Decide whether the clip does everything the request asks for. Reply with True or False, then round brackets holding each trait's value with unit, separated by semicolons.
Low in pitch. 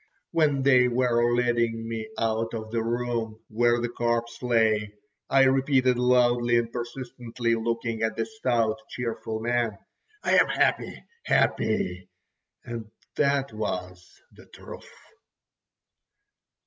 True (120 Hz)